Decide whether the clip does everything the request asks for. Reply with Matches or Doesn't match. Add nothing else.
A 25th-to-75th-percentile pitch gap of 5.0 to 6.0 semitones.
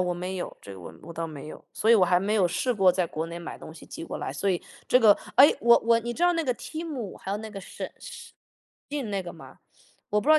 Matches